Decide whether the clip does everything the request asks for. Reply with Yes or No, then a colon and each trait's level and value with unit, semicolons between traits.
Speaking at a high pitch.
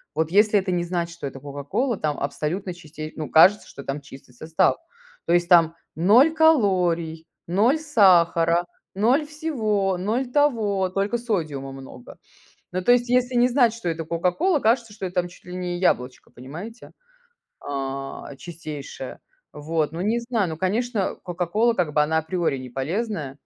No: medium, 180 Hz